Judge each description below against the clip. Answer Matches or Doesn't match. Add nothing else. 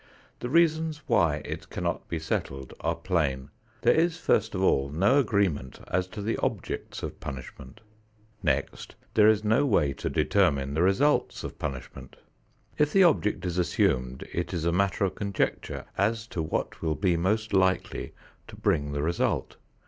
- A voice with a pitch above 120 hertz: Doesn't match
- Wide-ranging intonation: Matches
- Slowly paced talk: Doesn't match